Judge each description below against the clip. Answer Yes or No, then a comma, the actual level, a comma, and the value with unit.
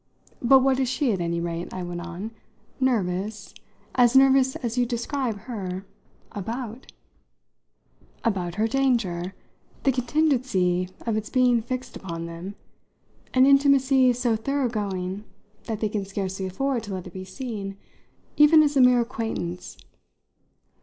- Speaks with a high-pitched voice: Yes, high, 225 Hz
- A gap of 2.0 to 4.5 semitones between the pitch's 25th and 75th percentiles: No, wide, 5.5 semitones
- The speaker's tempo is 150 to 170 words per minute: No, average, 140 wpm